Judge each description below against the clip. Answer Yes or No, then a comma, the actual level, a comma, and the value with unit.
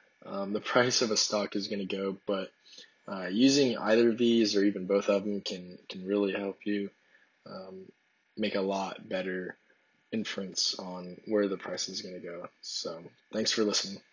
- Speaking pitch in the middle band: No, low, 100 Hz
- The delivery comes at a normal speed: Yes, average, 185 wpm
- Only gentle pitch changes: Yes, narrow, 1.9 semitones